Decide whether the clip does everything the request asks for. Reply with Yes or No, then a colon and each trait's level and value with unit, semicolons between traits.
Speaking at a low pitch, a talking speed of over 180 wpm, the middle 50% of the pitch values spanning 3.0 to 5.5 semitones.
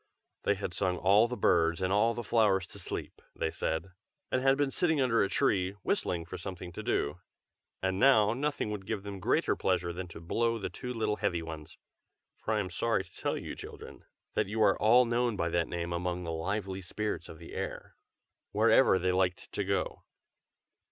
Yes: very low, 95 Hz; average, 200 wpm; average, 4.1 semitones